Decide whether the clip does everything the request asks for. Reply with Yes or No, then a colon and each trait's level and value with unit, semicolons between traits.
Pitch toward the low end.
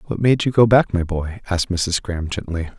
Yes: very low, 95 Hz